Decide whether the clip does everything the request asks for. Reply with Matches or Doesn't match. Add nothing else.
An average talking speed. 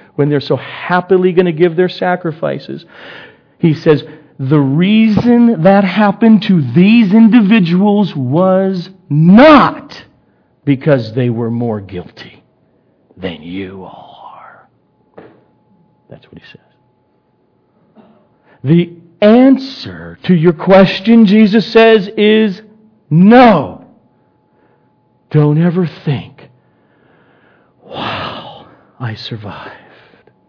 Doesn't match